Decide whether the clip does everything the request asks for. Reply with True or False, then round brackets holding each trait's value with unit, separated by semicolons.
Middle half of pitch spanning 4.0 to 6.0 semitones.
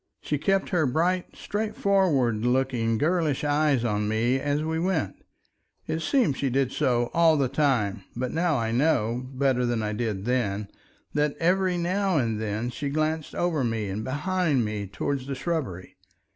True (5.5 semitones)